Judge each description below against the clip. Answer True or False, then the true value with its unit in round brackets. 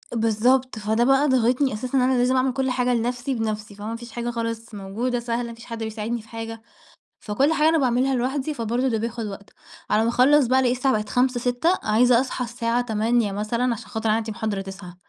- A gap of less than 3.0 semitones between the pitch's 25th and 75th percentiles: True (2.4 semitones)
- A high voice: True (235 Hz)